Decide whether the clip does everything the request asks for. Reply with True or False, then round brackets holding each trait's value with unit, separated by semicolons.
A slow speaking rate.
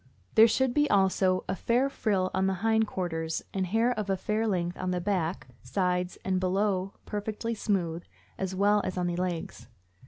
False (185 wpm)